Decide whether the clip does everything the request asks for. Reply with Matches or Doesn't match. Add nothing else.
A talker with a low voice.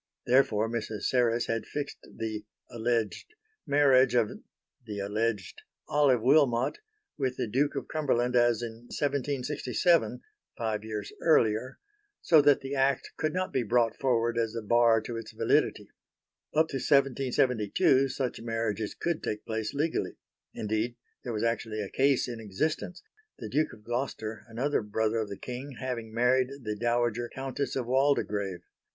Matches